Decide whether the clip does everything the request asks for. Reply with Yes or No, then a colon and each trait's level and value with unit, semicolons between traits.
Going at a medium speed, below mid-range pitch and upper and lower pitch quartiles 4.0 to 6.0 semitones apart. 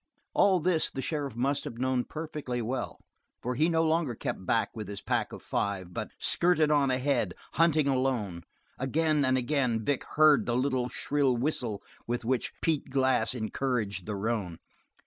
Yes: average, 165 wpm; low, 130 Hz; average, 4.3 semitones